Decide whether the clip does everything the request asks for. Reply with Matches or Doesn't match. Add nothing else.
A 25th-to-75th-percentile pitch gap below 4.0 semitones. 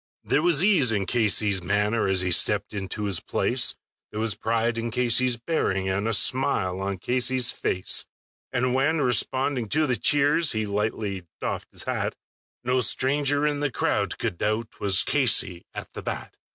Doesn't match